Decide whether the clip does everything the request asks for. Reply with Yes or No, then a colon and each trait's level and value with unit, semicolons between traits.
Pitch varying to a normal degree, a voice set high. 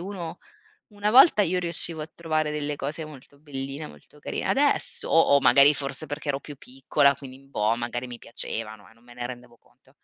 No: average, 4.1 semitones; medium, 140 Hz